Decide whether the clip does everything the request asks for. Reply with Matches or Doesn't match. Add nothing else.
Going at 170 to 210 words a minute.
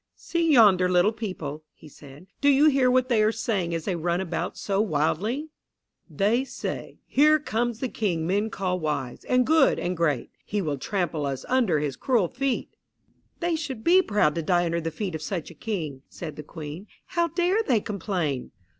Matches